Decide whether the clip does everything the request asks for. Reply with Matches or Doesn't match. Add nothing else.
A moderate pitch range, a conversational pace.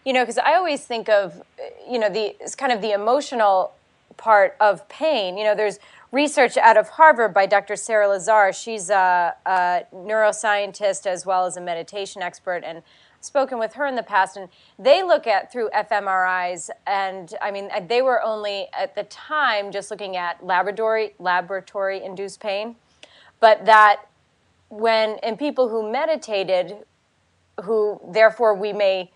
Matches